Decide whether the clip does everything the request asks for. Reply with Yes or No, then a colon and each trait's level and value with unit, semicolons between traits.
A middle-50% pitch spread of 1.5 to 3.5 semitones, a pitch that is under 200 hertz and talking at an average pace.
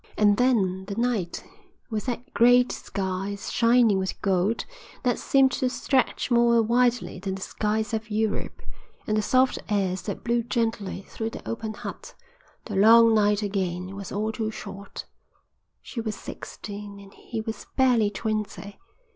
No: average, 2.8 semitones; high, 215 Hz; average, 155 wpm